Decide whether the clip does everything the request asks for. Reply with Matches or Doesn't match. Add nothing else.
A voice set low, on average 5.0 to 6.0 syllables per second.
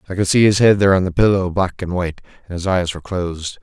Doesn't match